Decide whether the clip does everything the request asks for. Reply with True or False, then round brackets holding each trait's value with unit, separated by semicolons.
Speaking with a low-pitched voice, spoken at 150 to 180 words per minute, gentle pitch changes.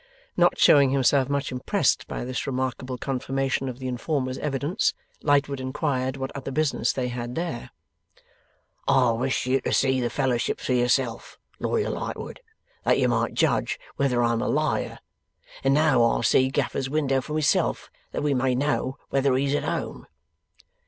True (130 Hz; 160 wpm; 1.7 semitones)